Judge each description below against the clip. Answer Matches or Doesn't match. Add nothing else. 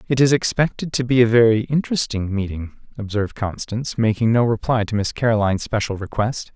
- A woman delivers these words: Doesn't match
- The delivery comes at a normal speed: Matches